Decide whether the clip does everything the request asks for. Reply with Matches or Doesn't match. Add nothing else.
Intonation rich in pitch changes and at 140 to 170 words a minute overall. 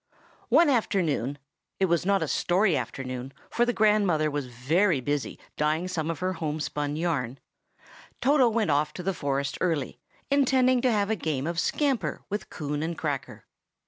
Matches